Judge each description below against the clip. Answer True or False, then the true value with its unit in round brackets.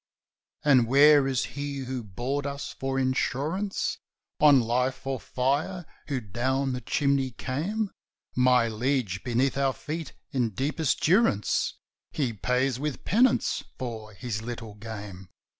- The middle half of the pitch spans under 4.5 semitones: True (3.1 semitones)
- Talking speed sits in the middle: False (130 wpm)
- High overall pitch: False (130 Hz)